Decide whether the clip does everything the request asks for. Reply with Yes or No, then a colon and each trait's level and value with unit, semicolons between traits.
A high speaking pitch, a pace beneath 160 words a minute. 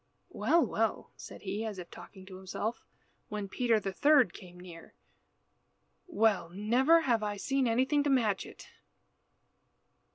Yes: high, 215 Hz; average, 150 wpm